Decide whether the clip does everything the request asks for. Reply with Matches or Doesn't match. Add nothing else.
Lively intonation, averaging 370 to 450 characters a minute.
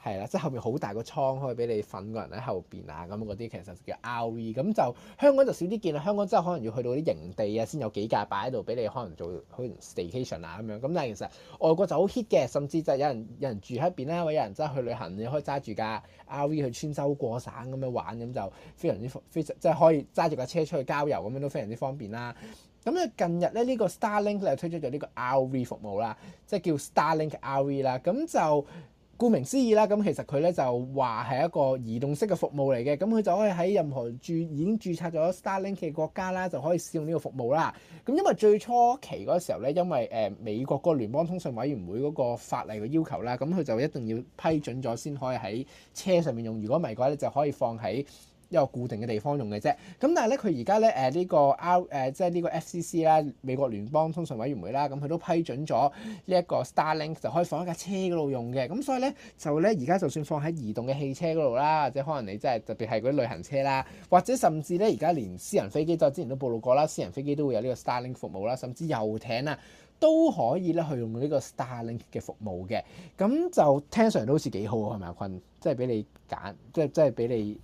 Matches